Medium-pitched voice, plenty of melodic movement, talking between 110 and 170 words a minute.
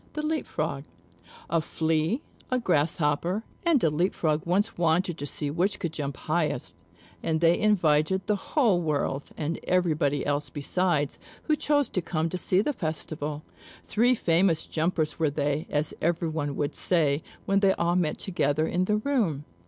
No: medium, 165 Hz; average, 4.0 semitones; average, 165 wpm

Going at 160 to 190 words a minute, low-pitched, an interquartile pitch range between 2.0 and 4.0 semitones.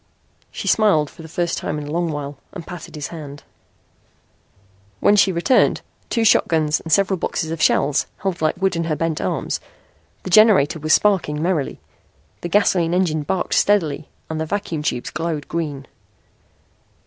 No: average, 165 wpm; medium, 165 Hz; average, 3.6 semitones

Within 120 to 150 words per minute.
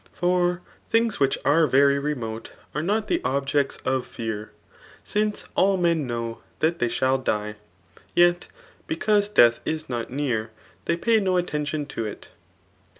Yes: average, 145 wpm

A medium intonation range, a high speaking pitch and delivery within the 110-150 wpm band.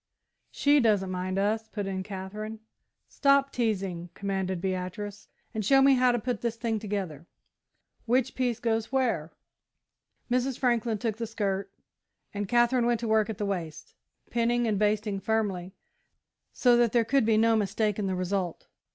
No: average, 3.5 semitones; high, 215 Hz; average, 160 wpm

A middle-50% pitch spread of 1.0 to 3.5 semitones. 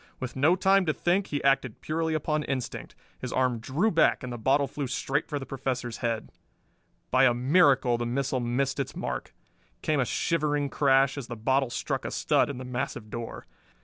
Yes: average, 2.9 semitones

